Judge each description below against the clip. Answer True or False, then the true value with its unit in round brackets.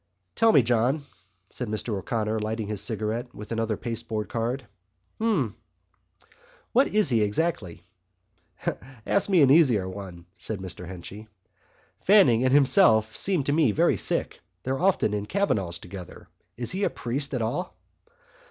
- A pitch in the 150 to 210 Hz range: False (115 Hz)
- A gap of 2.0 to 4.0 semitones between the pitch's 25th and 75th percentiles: False (5.4 semitones)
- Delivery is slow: False (145 wpm)